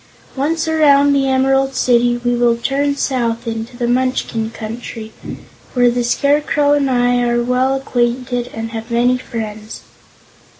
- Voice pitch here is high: Yes, high, 245 Hz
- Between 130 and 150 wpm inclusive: Yes, average, 140 wpm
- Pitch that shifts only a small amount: Yes, narrow, 2.3 semitones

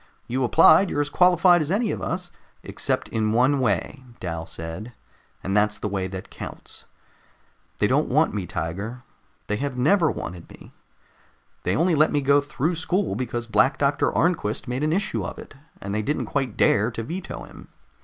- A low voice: Yes, low, 130 Hz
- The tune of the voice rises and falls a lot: Yes, wide, 7.2 semitones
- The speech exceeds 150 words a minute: Yes, average, 185 wpm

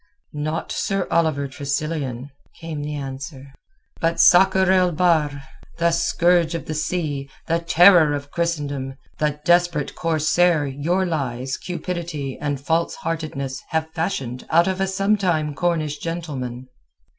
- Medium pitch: Yes, medium, 160 Hz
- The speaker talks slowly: Yes, slow, 130 wpm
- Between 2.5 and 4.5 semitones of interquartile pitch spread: Yes, average, 3.4 semitones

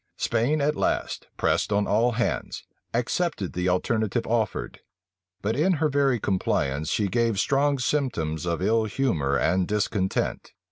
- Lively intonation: Yes, wide, 6.4 semitones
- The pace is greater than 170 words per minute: No, average, 145 wpm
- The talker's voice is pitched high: No, low, 110 Hz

